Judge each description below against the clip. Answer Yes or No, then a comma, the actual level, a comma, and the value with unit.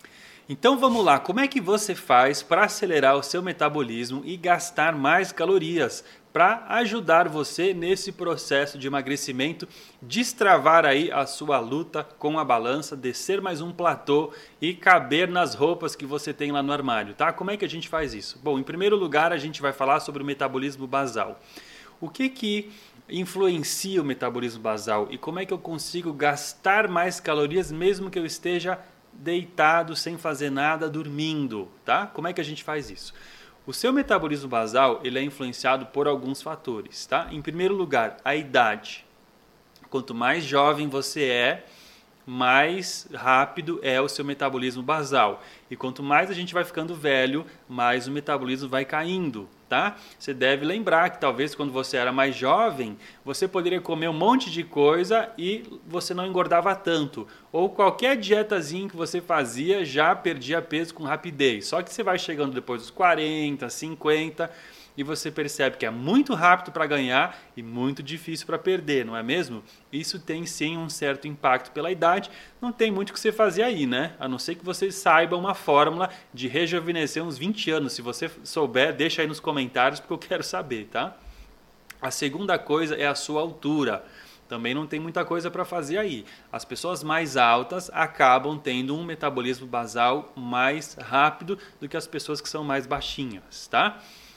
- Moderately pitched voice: Yes, medium, 155 Hz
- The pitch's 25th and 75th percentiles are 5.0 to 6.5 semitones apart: No, average, 4.1 semitones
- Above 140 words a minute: Yes, average, 175 wpm